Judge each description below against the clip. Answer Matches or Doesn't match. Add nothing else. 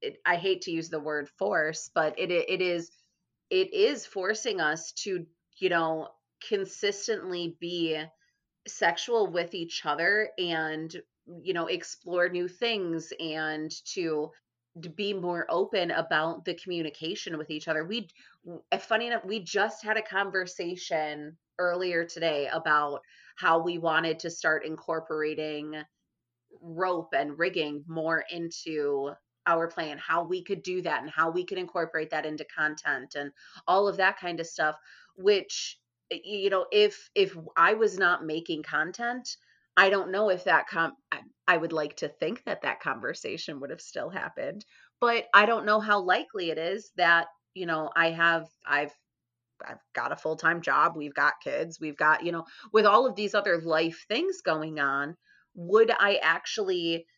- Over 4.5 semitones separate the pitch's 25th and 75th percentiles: Doesn't match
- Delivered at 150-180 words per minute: Matches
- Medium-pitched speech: Matches